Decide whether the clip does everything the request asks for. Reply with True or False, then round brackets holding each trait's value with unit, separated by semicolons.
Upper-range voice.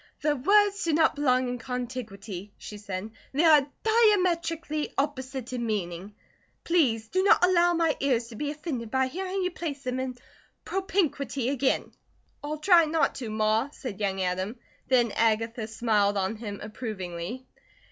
True (255 Hz)